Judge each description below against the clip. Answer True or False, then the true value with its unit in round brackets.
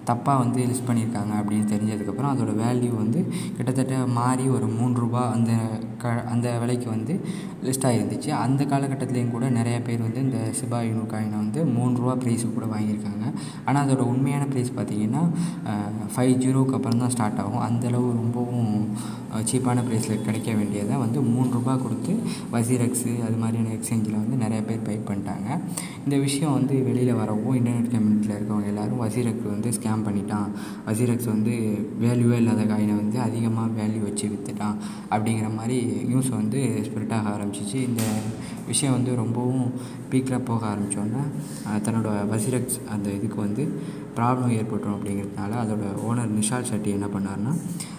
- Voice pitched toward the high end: False (115 Hz)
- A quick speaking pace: True (145 wpm)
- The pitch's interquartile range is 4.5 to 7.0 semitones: False (2.8 semitones)